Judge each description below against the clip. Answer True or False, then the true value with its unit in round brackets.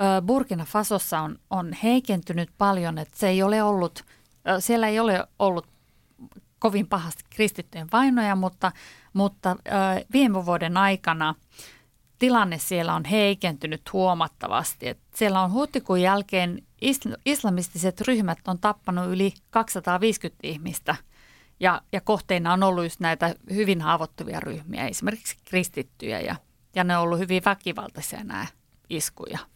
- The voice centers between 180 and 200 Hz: True (190 Hz)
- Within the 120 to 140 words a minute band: True (130 wpm)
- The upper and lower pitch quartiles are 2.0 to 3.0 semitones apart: False (3.4 semitones)